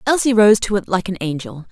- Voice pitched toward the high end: Yes, high, 200 Hz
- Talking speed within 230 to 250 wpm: Yes, fast, 245 wpm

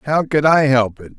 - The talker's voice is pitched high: No, low, 135 Hz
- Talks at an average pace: No, fast, 255 wpm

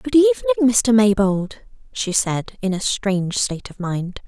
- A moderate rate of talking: Yes, average, 170 wpm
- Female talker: Yes, female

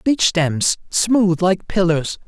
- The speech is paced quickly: No, slow, 130 wpm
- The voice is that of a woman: No, male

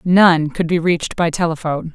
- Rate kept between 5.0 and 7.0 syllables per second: Yes, 5.4 syllables/s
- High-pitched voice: No, medium, 165 Hz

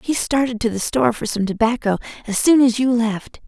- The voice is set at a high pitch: Yes, high, 230 Hz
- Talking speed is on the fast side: Yes, fast, 225 wpm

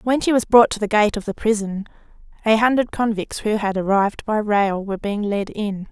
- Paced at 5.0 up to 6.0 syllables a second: Yes, 5.4 syllables/s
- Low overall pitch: No, high, 210 Hz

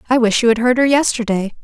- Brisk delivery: Yes, fast, 255 wpm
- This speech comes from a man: No, female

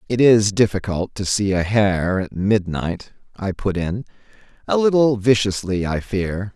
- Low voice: Yes, low, 100 Hz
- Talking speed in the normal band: Yes, average, 155 wpm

